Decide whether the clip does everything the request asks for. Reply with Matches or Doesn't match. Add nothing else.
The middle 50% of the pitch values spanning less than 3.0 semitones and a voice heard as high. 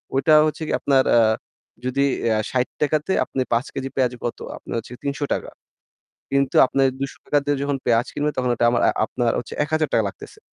Doesn't match